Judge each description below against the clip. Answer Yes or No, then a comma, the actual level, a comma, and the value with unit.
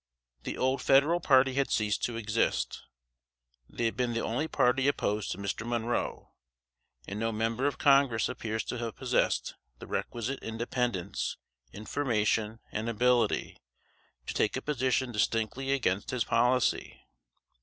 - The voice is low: Yes, low, 120 Hz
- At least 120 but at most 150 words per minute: Yes, average, 140 wpm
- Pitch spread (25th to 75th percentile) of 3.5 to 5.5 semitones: No, average, 2.8 semitones